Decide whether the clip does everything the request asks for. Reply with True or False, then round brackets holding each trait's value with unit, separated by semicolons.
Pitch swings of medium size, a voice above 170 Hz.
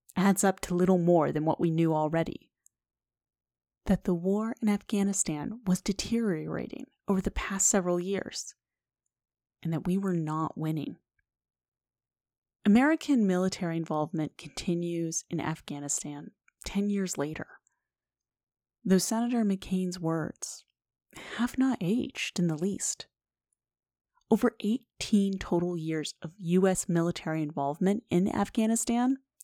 True (4.0 semitones; 185 Hz)